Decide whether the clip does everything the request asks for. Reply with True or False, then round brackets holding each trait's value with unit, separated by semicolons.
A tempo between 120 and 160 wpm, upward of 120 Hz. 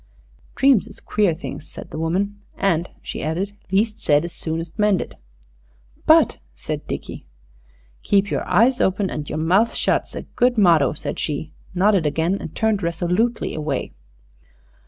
True (155 wpm; 185 Hz)